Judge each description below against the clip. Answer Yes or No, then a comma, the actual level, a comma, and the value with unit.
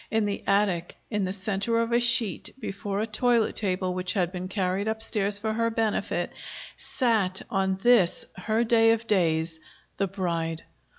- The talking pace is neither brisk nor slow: Yes, average, 165 wpm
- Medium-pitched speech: No, high, 200 Hz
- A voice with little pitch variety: No, average, 3.4 semitones